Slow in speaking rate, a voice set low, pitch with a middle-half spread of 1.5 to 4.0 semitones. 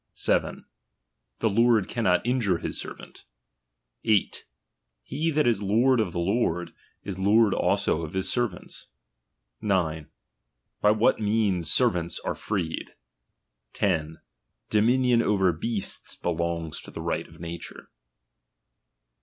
No: slow, 120 wpm; low, 100 Hz; average, 5.1 semitones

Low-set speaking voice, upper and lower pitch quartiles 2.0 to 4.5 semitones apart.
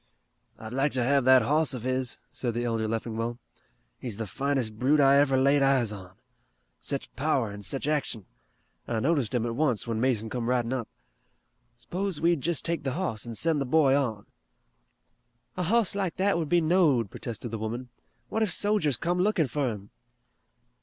No: low, 130 Hz; average, 5.1 semitones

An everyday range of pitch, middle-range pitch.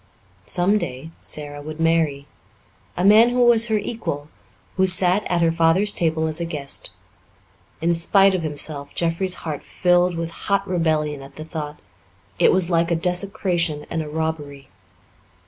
Yes: average, 3.2 semitones; medium, 165 Hz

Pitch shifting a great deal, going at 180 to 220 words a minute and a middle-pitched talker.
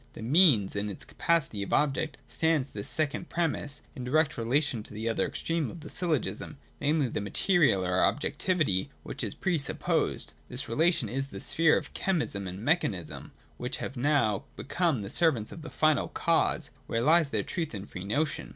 Yes: wide, 6.9 semitones; average, 190 wpm; medium, 145 Hz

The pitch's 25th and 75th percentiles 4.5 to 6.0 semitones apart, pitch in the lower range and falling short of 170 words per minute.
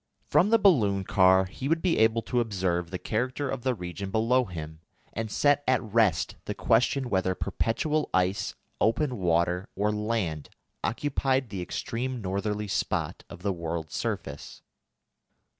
Yes: wide, 5.4 semitones; low, 105 Hz; average, 150 wpm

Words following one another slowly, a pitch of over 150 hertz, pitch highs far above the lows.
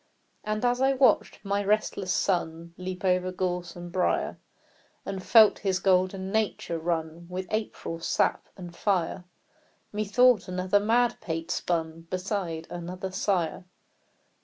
No: slow, 125 wpm; medium, 185 Hz; average, 2.7 semitones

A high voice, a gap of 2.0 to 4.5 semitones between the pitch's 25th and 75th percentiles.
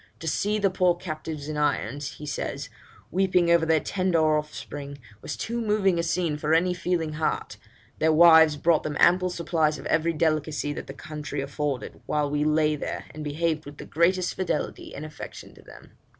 No: medium, 155 Hz; narrow, 2.5 semitones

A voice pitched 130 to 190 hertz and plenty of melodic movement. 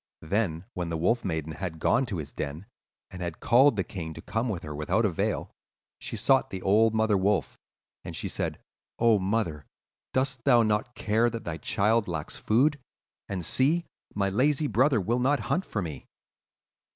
No: low, 105 Hz; wide, 5.8 semitones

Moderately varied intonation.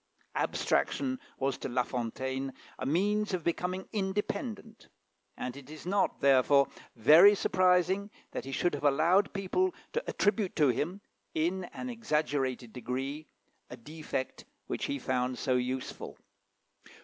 No: wide, 6.9 semitones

